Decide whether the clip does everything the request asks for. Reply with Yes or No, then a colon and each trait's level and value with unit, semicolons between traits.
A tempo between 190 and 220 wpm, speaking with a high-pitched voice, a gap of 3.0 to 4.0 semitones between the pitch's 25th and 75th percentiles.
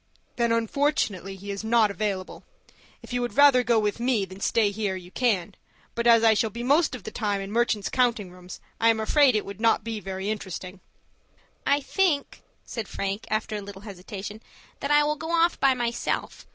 Yes: average, 200 wpm; high, 220 Hz; average, 3.6 semitones